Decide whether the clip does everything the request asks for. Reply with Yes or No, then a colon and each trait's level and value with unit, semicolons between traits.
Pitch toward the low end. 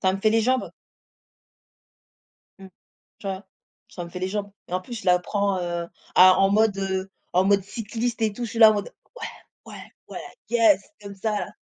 No: high, 200 Hz